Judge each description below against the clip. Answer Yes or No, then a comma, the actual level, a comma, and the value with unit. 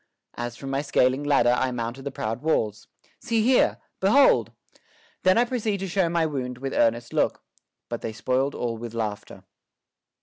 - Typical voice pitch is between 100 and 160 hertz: Yes, low, 135 Hz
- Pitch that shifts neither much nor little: No, wide, 6.4 semitones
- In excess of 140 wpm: Yes, average, 170 wpm